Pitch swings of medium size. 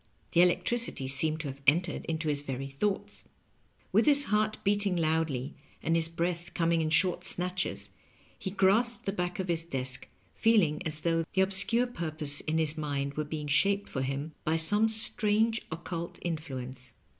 Yes: average, 4.4 semitones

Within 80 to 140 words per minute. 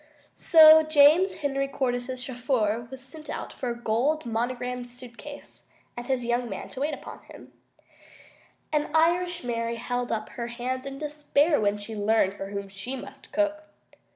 No: average, 155 wpm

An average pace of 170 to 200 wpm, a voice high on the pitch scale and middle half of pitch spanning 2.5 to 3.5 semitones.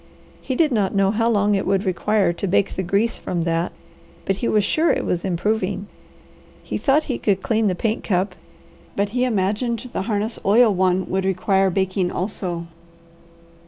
Yes: average, 180 wpm; high, 200 Hz; average, 2.8 semitones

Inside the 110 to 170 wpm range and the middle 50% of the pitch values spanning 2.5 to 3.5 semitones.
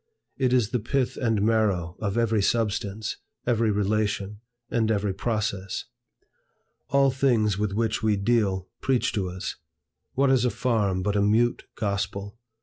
Yes: average, 145 wpm; average, 2.9 semitones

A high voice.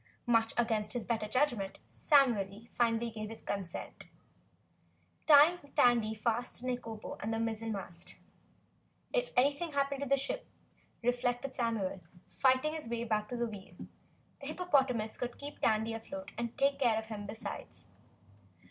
Yes: high, 235 Hz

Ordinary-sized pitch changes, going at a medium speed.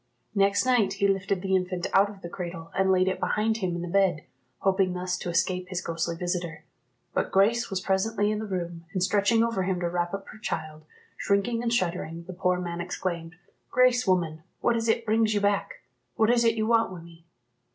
No: average, 3.3 semitones; fast, 215 wpm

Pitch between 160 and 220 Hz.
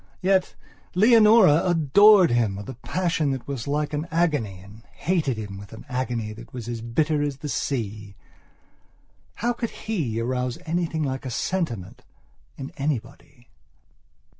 No: low, 135 Hz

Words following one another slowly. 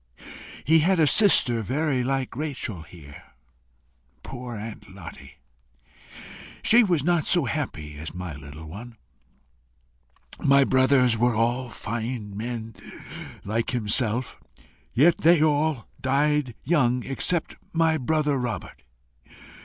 Yes: slow, 115 wpm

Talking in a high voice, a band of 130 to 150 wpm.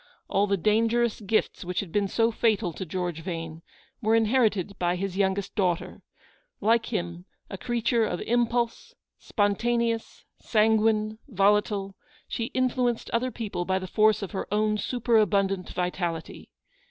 Yes: high, 210 Hz; average, 140 wpm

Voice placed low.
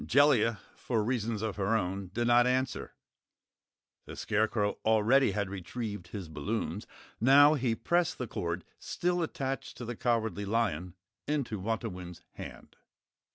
Yes: low, 110 Hz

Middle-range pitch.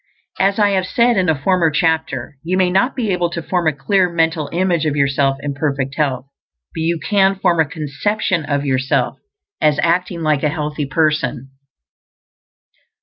Yes: medium, 160 Hz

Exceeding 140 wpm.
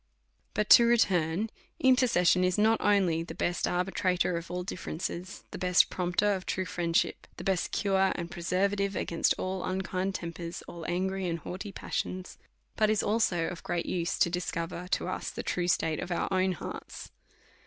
Yes: average, 175 wpm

